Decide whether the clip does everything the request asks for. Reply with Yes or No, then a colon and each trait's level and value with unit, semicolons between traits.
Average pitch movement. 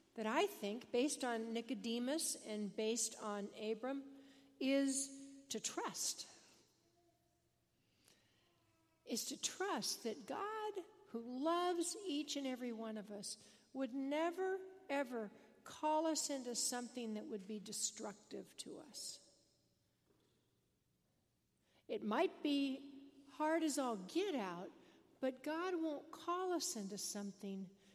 No: wide, 6.3 semitones